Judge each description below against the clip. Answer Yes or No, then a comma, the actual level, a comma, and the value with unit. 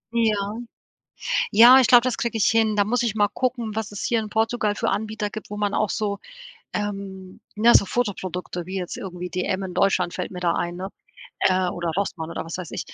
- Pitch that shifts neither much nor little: Yes, average, 3.1 semitones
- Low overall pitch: No, high, 205 Hz